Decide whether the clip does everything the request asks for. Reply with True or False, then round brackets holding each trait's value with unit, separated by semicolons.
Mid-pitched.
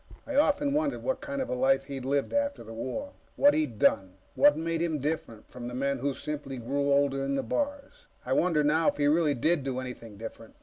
True (145 Hz)